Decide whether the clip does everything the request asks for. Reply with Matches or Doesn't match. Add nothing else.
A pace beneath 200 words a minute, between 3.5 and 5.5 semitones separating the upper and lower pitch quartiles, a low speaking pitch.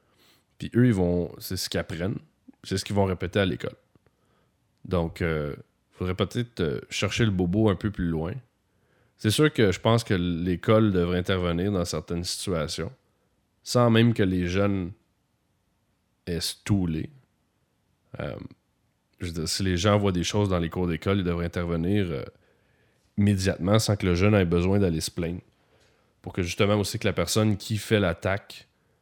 Doesn't match